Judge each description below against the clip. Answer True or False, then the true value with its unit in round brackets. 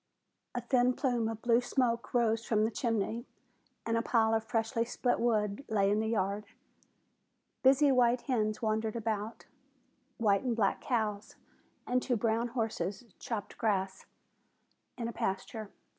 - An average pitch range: False (2.1 semitones)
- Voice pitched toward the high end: True (225 Hz)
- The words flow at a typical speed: True (145 wpm)